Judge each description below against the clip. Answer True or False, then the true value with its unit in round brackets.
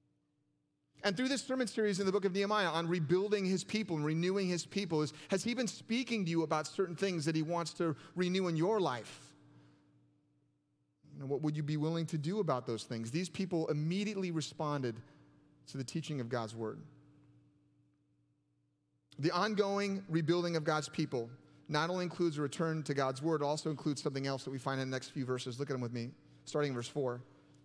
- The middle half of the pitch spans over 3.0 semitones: True (5.5 semitones)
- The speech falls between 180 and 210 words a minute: True (200 wpm)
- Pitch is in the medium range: True (155 Hz)